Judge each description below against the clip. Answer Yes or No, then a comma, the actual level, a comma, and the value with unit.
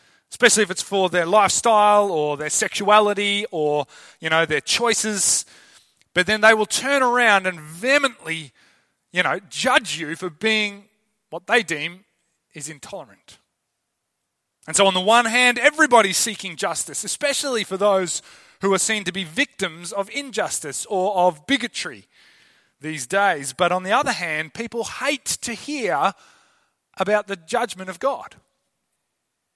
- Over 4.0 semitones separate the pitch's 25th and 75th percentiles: Yes, average, 4.6 semitones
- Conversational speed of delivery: Yes, average, 145 wpm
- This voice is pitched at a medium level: No, high, 205 Hz